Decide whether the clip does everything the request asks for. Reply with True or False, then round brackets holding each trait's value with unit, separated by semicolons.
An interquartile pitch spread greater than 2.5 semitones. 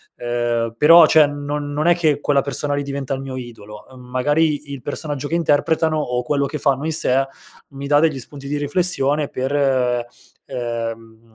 True (2.9 semitones)